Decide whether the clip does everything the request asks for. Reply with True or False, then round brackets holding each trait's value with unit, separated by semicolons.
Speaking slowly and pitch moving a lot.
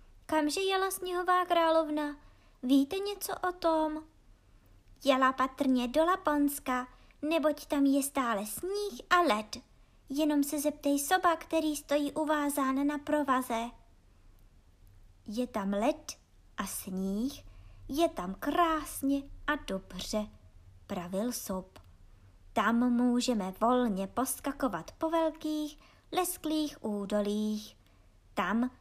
True (100 wpm; 7.0 semitones)